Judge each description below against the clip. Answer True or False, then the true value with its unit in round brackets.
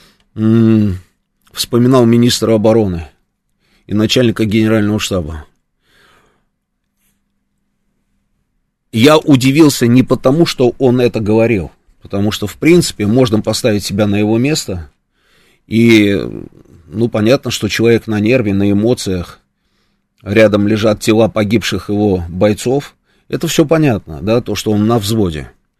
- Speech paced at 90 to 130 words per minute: True (115 wpm)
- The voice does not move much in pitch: False (3.0 semitones)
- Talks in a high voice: False (110 Hz)